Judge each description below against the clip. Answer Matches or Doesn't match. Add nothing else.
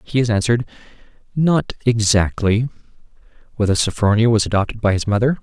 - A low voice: Matches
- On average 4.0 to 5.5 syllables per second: Doesn't match